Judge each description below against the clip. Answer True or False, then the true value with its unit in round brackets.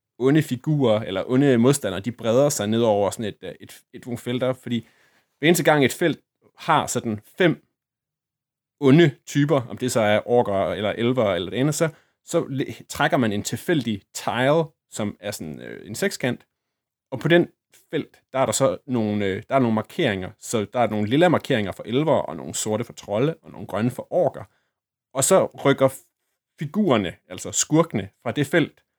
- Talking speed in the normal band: True (185 wpm)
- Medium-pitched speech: False (130 Hz)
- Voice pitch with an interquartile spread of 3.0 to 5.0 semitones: True (4.6 semitones)